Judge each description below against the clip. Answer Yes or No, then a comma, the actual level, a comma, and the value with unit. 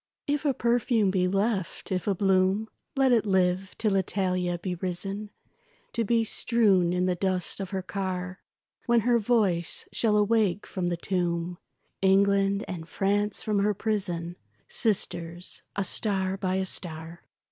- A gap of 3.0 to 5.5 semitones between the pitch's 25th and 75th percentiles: No, narrow, 2.6 semitones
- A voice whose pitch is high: Yes, high, 195 Hz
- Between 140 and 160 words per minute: Yes, average, 150 wpm